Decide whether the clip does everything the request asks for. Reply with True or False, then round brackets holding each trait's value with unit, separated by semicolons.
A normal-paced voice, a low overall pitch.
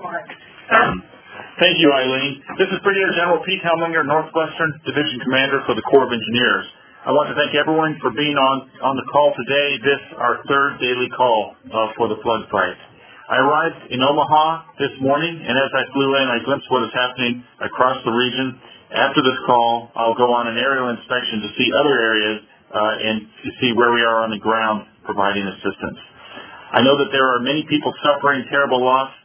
True (190 wpm; 130 Hz)